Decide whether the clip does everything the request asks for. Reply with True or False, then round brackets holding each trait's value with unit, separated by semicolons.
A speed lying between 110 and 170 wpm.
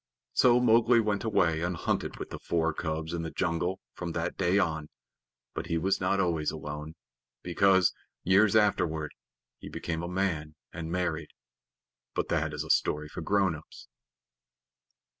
True (160 wpm)